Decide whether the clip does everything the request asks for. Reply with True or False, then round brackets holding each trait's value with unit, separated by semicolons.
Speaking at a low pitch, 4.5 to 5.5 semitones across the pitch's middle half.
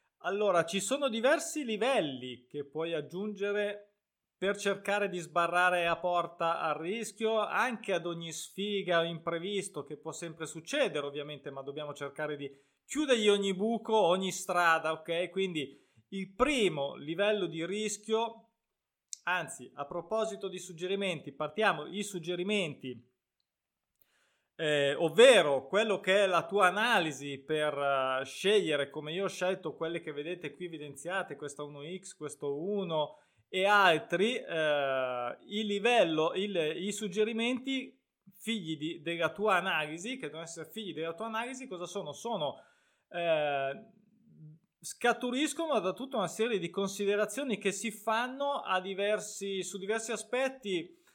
False (185 Hz; 5.0 semitones)